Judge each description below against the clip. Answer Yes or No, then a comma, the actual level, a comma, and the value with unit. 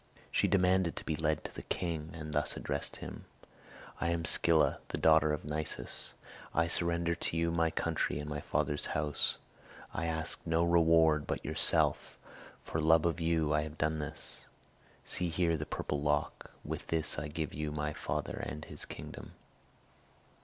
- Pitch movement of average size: No, narrow, 1.7 semitones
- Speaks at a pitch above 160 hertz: No, very low, 80 Hz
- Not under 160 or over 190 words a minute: Yes, average, 170 wpm